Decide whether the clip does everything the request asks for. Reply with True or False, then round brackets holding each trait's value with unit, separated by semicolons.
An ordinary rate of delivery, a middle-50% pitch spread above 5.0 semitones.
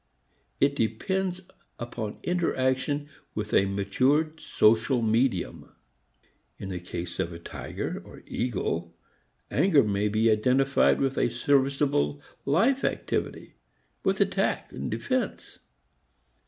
False (110 wpm; 5.4 semitones)